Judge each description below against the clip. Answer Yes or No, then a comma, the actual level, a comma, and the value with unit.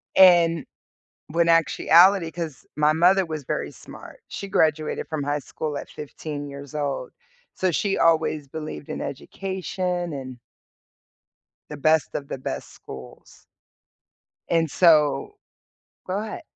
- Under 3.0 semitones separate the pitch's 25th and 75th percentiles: No, average, 3.3 semitones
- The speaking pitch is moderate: Yes, medium, 160 Hz